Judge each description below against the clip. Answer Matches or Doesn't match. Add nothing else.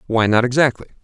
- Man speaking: Matches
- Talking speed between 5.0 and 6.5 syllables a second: Doesn't match